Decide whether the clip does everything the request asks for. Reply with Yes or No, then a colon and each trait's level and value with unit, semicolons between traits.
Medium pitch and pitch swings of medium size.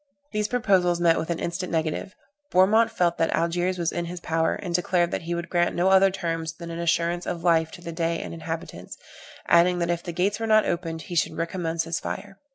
No: medium, 170 Hz; narrow, 1.5 semitones